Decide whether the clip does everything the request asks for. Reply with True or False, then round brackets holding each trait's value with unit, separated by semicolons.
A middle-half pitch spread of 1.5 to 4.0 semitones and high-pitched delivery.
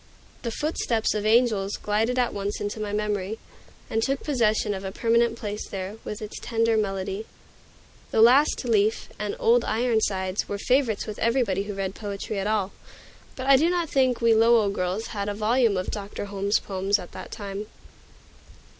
True (2.6 semitones; 215 Hz)